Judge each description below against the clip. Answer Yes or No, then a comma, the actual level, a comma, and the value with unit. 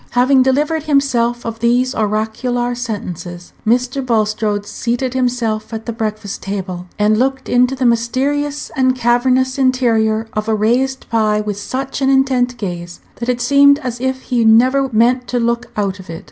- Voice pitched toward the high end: Yes, high, 240 Hz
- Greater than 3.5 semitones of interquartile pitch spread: No, average, 3.1 semitones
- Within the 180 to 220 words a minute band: No, average, 165 wpm